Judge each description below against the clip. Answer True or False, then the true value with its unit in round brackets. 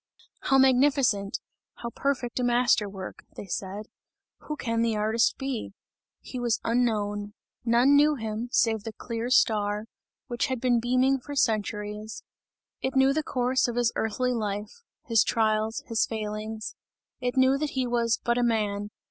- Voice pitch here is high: True (235 Hz)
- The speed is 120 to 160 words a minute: True (155 wpm)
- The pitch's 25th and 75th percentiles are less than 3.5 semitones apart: True (3.0 semitones)